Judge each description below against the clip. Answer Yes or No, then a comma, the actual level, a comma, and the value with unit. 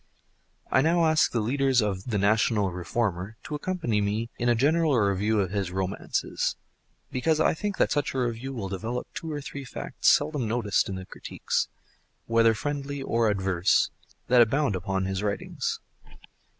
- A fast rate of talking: No, average, 160 wpm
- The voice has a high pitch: No, low, 115 Hz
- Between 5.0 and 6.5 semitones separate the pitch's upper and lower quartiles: Yes, wide, 5.6 semitones